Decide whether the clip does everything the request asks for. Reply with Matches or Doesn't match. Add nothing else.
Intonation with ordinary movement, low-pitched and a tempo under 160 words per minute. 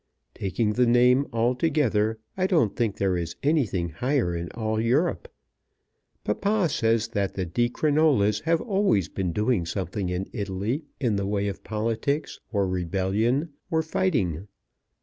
Doesn't match